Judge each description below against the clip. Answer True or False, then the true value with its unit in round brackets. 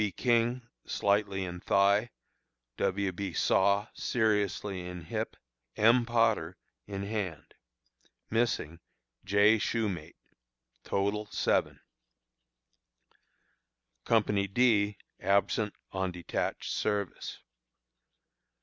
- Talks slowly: True (85 wpm)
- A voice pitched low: True (100 Hz)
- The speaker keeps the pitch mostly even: True (2.3 semitones)